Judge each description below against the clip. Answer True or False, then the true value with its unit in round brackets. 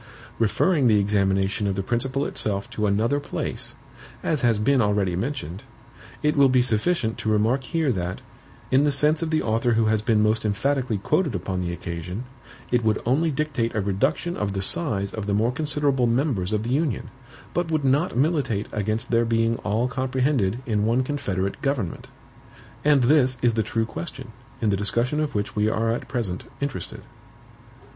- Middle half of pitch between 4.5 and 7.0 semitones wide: True (5.0 semitones)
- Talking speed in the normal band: True (180 wpm)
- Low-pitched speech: True (115 Hz)